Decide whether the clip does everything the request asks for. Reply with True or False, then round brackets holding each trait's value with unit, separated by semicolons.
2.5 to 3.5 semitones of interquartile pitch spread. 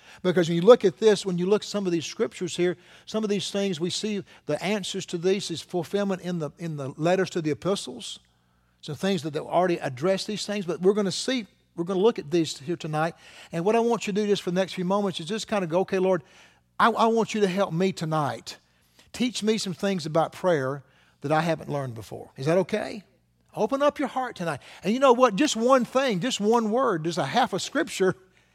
False (4.3 semitones)